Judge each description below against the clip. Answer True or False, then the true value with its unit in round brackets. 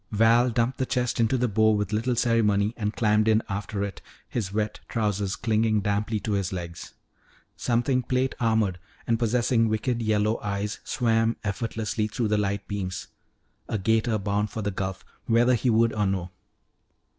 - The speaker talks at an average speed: True (170 wpm)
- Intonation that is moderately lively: False (2.1 semitones)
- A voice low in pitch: True (110 Hz)